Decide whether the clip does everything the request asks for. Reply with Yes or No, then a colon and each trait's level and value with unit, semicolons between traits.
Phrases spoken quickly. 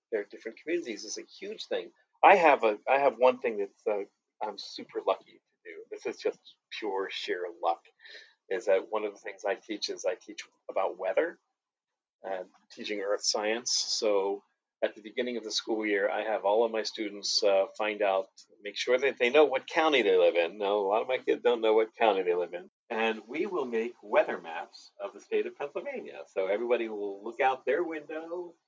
Yes: fast, 215 wpm